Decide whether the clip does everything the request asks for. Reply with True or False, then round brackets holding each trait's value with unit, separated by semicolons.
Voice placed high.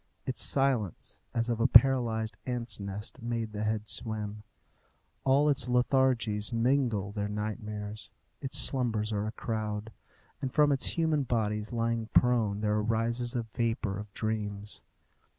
False (115 Hz)